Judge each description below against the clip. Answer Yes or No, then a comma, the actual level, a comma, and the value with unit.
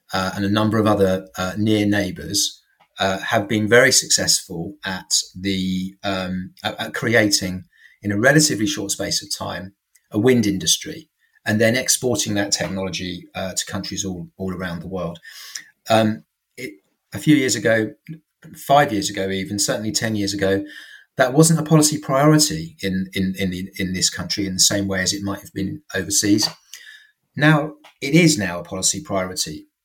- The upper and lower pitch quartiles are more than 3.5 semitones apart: Yes, average, 5.2 semitones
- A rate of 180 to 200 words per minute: No, average, 170 wpm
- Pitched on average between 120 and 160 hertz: No, low, 100 Hz